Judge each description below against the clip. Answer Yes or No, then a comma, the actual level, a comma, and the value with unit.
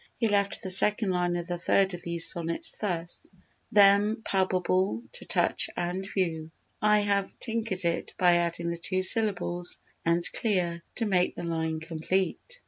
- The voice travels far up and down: No, average, 2.9 semitones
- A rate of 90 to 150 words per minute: No, average, 160 wpm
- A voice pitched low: No, medium, 185 Hz